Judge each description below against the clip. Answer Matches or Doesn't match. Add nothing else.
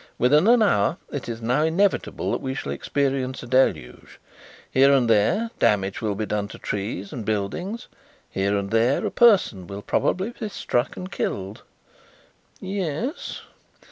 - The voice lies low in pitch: Matches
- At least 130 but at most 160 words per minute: Matches